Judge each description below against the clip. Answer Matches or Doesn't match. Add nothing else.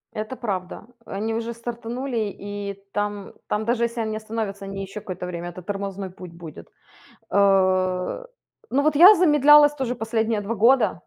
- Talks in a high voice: Matches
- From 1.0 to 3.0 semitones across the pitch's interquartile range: Doesn't match